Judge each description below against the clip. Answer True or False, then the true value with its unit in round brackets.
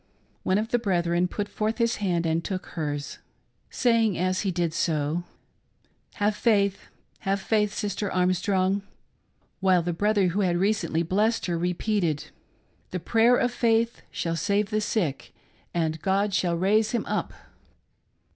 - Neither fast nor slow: True (165 wpm)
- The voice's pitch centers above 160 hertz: True (190 Hz)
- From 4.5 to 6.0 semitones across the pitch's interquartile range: False (3.6 semitones)